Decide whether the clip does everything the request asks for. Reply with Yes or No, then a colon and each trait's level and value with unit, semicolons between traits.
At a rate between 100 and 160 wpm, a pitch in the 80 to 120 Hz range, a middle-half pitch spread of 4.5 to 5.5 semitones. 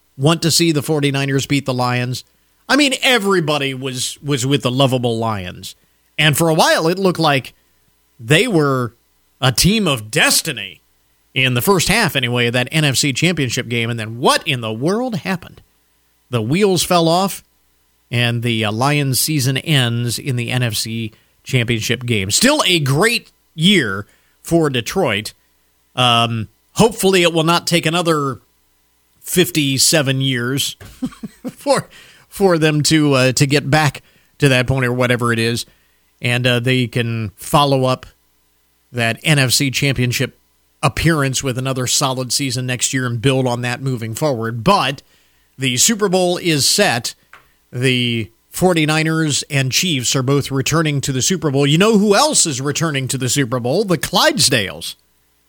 No: average, 155 wpm; low, 135 Hz; average, 5.0 semitones